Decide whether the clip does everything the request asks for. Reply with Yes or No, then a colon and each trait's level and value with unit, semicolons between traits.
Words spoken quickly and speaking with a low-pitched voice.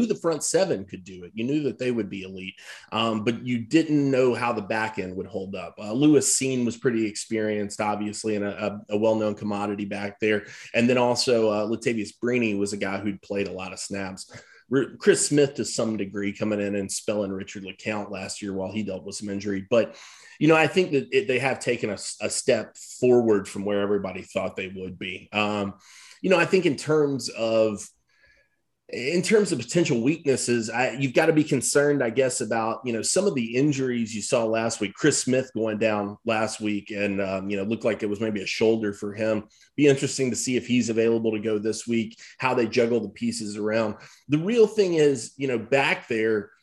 Yes: fast, 220 wpm; low, 110 Hz